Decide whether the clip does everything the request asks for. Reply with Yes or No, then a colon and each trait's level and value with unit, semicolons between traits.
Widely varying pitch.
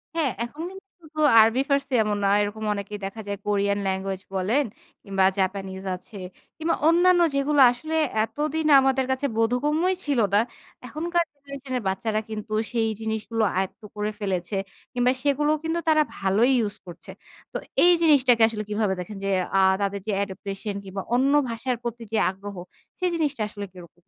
Yes: wide, 6.2 semitones